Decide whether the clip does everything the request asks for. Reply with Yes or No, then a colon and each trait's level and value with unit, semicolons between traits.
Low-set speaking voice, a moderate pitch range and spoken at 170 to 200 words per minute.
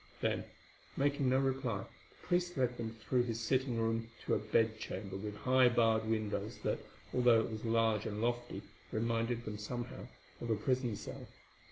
No: low, 115 Hz; narrow, 2.2 semitones; average, 175 wpm